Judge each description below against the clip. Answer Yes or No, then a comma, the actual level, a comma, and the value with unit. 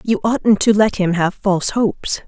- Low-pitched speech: No, high, 205 Hz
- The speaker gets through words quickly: Yes, fast, 210 wpm